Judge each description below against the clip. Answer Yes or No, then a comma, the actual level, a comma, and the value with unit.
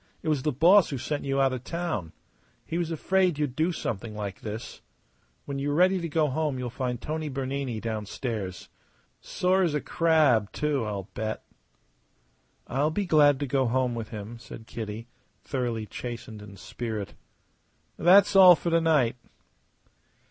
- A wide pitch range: Yes, wide, 5.8 semitones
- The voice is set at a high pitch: No, low, 135 Hz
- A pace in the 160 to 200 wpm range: Yes, average, 165 wpm